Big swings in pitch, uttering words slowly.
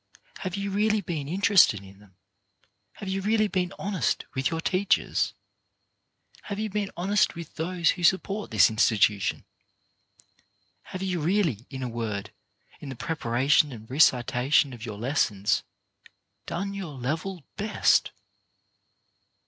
Yes: wide, 8.2 semitones; slow, 130 wpm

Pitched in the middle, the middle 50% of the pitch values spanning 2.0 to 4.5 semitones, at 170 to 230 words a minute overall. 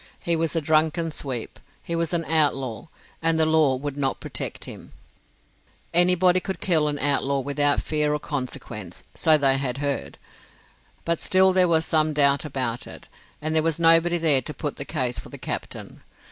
Yes: medium, 155 Hz; average, 2.9 semitones; average, 180 wpm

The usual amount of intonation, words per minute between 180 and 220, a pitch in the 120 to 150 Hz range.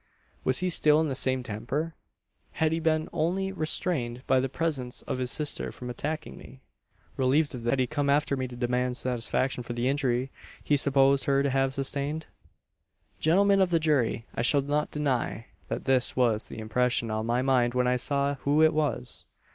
Yes: average, 3.5 semitones; average, 195 wpm; low, 135 Hz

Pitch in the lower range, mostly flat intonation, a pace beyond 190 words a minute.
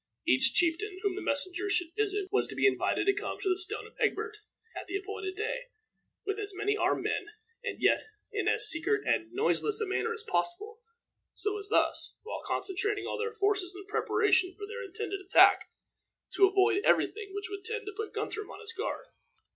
No: very high, 405 Hz; narrow, 2.1 semitones; average, 200 wpm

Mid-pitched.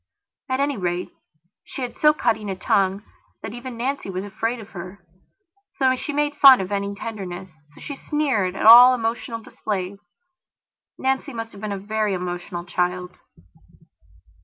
No: high, 215 Hz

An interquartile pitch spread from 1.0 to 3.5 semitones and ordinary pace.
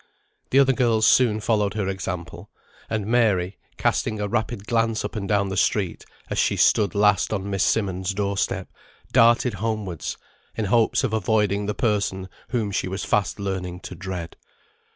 Yes: narrow, 2.5 semitones; average, 170 wpm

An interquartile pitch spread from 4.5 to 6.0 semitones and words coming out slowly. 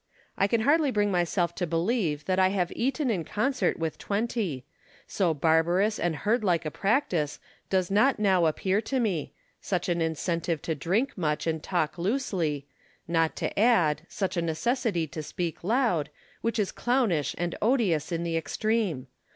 No: average, 5.1 semitones; average, 165 wpm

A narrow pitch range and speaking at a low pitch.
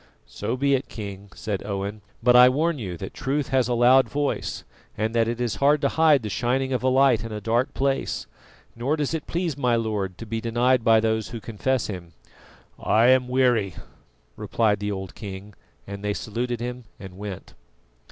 No: average, 3.9 semitones; low, 120 Hz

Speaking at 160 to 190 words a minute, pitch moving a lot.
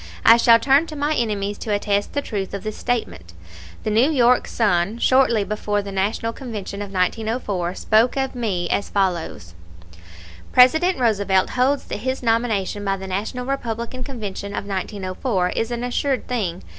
No: average, 165 wpm; average, 4.0 semitones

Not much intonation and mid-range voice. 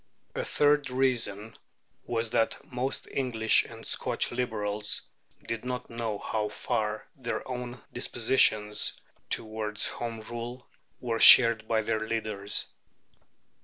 No: narrow, 2.3 semitones; low, 115 Hz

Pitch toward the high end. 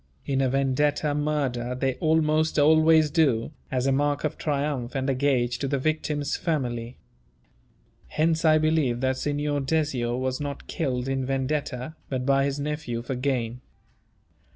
No: medium, 140 Hz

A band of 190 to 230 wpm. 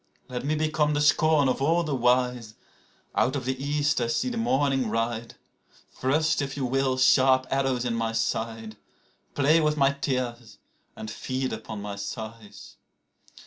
No: average, 160 wpm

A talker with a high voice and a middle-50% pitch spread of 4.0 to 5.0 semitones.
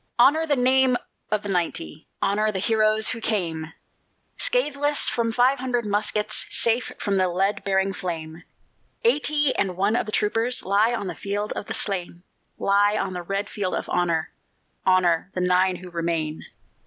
Yes: high, 205 Hz; average, 4.4 semitones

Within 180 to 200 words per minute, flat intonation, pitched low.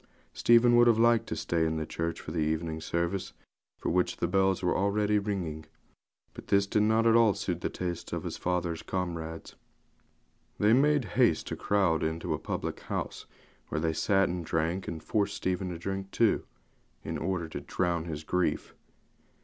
No: average, 185 wpm; average, 3.8 semitones; very low, 90 Hz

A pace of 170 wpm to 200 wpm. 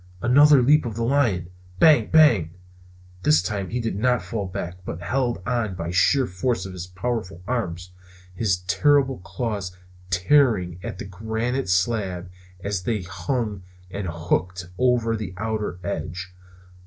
No: average, 145 wpm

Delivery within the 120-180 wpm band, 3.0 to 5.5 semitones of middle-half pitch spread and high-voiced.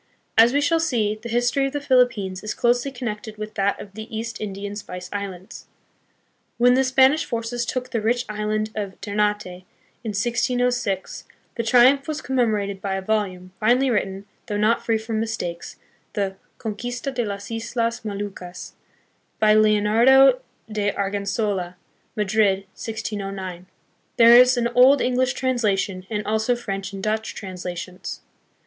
Yes: average, 150 wpm; average, 3.4 semitones; high, 215 Hz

